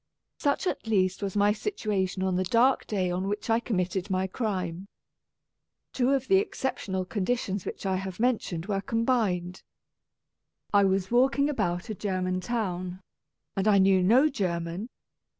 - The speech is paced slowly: No, average, 150 wpm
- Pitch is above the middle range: Yes, high, 195 Hz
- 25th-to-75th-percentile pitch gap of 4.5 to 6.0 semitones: No, average, 3.9 semitones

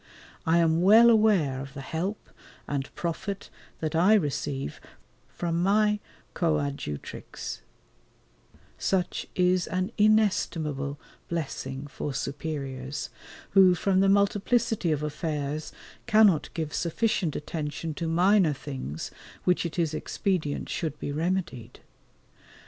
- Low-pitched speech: No, medium, 165 Hz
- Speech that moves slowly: Yes, slow, 110 wpm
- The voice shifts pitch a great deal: No, average, 4.9 semitones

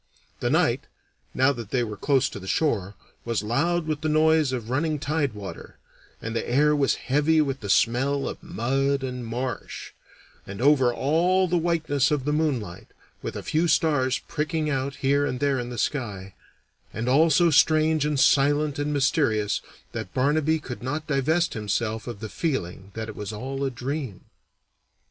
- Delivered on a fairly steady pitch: No, average, 4.3 semitones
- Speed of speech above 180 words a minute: No, average, 175 wpm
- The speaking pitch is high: No, low, 135 Hz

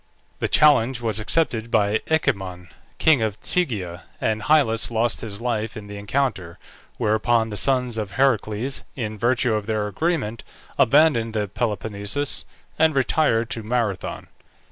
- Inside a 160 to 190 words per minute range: No, average, 140 wpm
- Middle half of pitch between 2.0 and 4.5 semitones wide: Yes, average, 3.7 semitones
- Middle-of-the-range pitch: No, low, 115 Hz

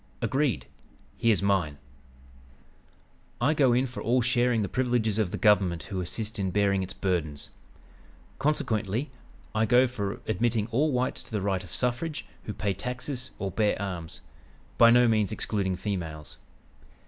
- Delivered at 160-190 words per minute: No, average, 150 wpm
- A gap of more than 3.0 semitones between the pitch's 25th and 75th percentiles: Yes, average, 4.1 semitones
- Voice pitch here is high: No, low, 110 Hz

